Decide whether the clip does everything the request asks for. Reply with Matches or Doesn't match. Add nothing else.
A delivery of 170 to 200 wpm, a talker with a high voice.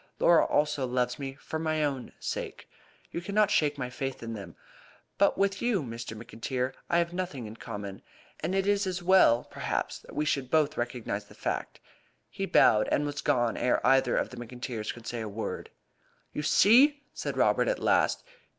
Doesn't match